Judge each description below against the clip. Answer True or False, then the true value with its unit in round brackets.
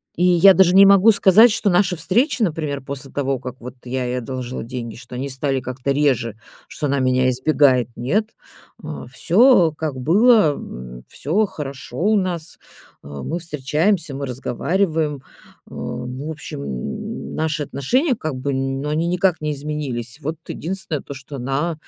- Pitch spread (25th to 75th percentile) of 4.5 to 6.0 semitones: True (5.3 semitones)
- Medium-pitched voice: True (145 Hz)